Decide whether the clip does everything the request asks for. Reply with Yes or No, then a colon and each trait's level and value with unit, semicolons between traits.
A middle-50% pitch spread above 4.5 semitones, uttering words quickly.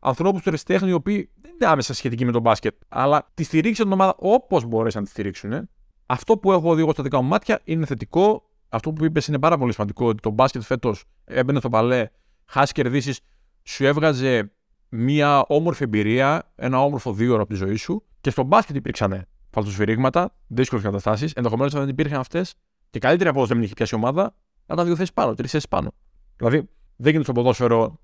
Yes: wide, 5.5 semitones; fast, 195 wpm